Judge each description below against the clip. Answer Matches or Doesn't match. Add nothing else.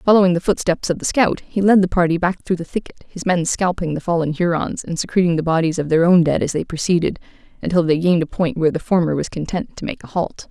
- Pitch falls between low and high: Matches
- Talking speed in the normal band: Doesn't match